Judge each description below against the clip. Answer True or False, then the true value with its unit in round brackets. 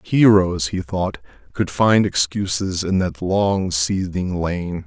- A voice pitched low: True (90 Hz)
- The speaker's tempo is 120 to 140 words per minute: True (135 wpm)